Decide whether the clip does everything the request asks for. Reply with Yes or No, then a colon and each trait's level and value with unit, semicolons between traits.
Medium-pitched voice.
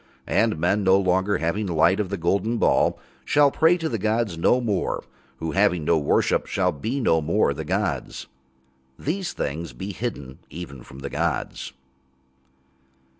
No: very low, 95 Hz